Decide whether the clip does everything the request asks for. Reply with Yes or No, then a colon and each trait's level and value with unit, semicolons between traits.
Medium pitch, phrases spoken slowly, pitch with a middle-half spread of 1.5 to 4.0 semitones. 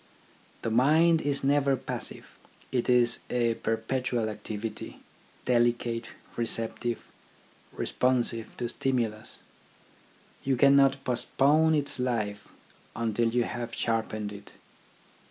No: low, 120 Hz; slow, 100 wpm; average, 2.8 semitones